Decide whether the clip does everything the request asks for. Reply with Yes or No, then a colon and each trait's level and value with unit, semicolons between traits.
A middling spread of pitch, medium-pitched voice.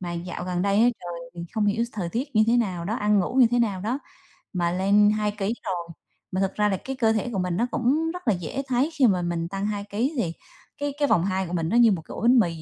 No: average, 4.9 semitones; high, 205 Hz